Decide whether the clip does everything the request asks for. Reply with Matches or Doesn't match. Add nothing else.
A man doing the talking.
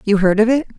Doesn't match